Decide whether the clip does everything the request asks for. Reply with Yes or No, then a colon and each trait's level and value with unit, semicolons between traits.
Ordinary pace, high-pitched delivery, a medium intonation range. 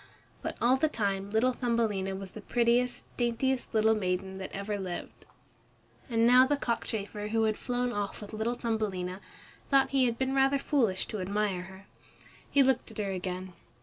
Yes: average, 175 wpm; high, 220 Hz; average, 4.1 semitones